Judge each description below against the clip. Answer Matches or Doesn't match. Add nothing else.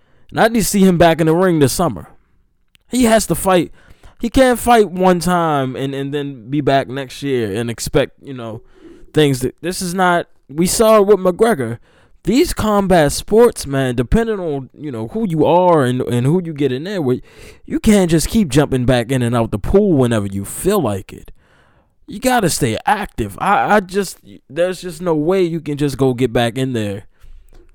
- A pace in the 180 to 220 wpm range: Matches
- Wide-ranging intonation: Matches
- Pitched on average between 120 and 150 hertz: Doesn't match